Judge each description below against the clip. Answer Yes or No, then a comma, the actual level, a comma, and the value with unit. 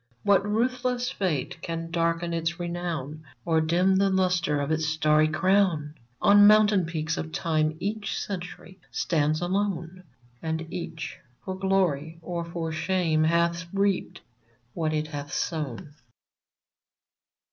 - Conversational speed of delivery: No, slow, 125 wpm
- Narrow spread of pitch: No, average, 3.2 semitones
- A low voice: No, medium, 170 Hz